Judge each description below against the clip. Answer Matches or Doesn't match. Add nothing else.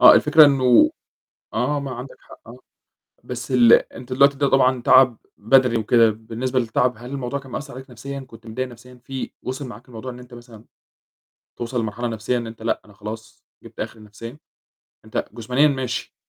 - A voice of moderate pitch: Doesn't match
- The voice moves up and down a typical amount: Doesn't match